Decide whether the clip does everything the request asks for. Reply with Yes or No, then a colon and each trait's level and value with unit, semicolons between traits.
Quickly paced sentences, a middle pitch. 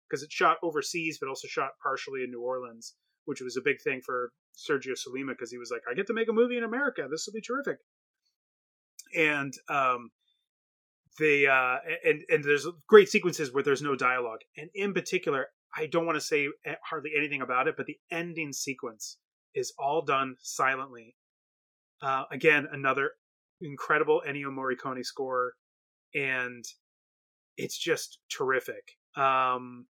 No: average, 160 wpm; medium, 145 Hz